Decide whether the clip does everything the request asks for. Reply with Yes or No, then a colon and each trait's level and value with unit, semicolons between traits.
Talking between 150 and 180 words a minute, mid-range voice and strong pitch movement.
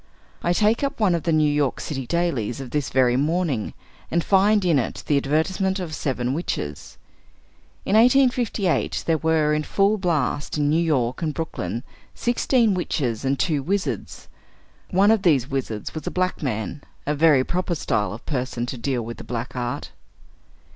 Yes: average, 175 wpm; medium, 155 Hz; wide, 6.0 semitones